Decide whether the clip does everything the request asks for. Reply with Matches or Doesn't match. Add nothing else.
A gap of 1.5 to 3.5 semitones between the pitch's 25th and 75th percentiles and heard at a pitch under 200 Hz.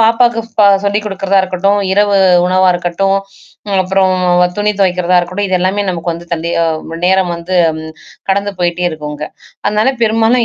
Matches